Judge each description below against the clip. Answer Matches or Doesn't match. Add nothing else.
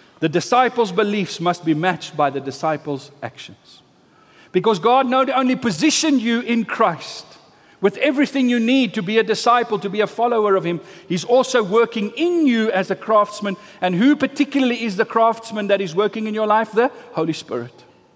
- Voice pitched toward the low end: Doesn't match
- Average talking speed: Matches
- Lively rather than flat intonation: Doesn't match